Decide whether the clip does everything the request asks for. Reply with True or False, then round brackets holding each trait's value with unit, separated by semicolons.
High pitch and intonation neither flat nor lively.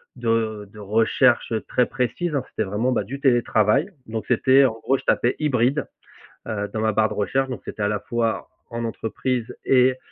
False (120 Hz; 3.1 semitones)